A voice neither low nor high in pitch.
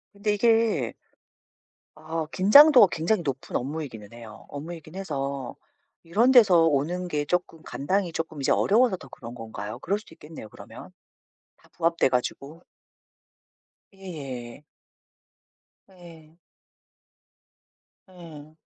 Yes: medium, 165 Hz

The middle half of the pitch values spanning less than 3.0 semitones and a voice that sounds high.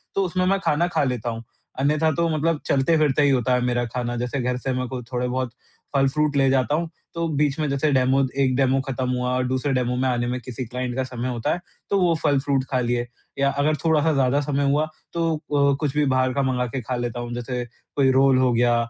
No: narrow, 2.6 semitones; low, 130 Hz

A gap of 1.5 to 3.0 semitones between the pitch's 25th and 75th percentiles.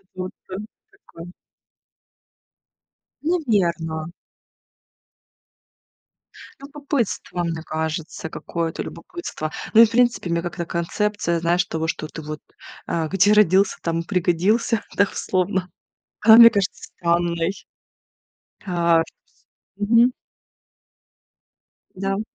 No: average, 4.1 semitones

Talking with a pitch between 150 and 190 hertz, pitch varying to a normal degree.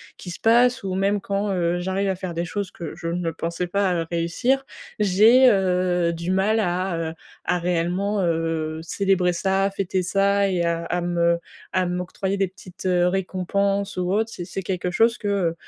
No: medium, 185 Hz; narrow, 2.3 semitones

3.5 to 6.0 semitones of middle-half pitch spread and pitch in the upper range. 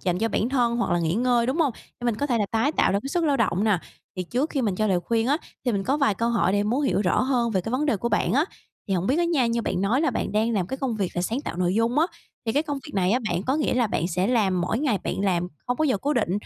Yes: average, 5.3 semitones; high, 230 Hz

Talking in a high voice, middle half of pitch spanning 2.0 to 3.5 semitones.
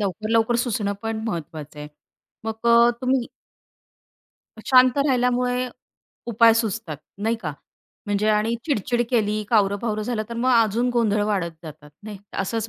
Yes: high, 225 Hz; average, 2.7 semitones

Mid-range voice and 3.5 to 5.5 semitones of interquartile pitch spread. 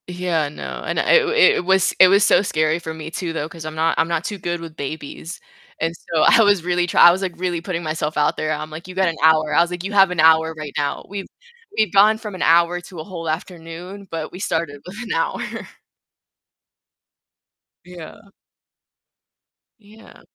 No: medium, 170 Hz; average, 2.7 semitones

